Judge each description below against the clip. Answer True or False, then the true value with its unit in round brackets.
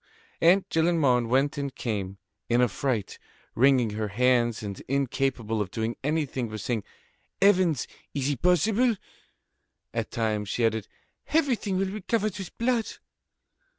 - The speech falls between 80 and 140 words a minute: True (135 wpm)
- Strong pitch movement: True (8.0 semitones)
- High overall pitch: False (130 Hz)